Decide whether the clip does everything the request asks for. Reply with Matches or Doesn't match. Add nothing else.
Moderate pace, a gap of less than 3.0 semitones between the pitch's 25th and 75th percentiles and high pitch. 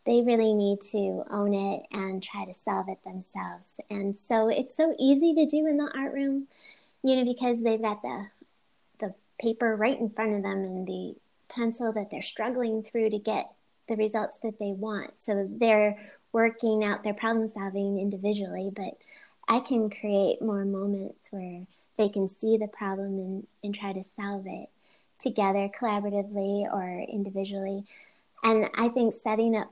Matches